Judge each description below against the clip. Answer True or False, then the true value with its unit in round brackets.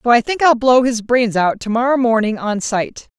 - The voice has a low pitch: False (235 Hz)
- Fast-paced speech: True (225 wpm)